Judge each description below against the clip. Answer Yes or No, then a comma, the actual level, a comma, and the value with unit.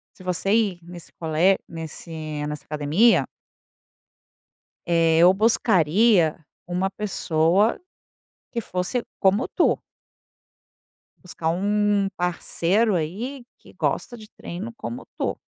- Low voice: No, medium, 185 Hz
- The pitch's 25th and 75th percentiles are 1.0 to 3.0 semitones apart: No, average, 4.2 semitones